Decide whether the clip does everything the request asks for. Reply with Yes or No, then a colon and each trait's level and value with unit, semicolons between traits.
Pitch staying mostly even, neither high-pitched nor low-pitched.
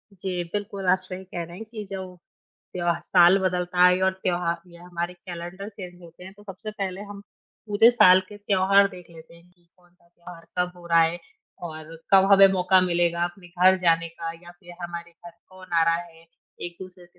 Yes: narrow, 1.7 semitones; medium, 180 Hz